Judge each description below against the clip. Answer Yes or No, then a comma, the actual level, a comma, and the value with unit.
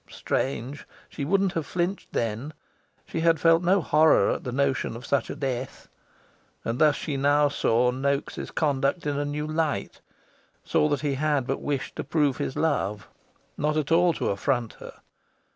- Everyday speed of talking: Yes, average, 175 wpm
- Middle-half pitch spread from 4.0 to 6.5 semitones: No, average, 2.8 semitones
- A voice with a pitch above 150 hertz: No, medium, 145 Hz